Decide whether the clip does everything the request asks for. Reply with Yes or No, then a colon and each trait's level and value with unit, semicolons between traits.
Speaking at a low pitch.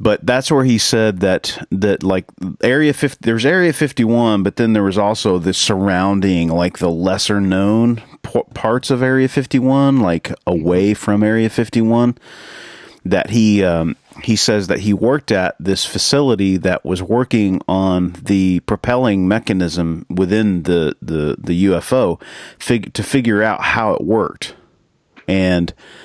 Yes: low, 105 Hz